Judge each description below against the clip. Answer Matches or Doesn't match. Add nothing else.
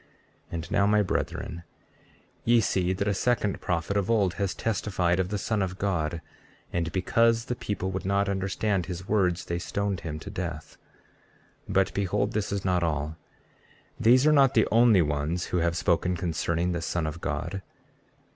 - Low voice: Matches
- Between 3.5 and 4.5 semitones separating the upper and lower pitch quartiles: Doesn't match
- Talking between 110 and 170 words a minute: Doesn't match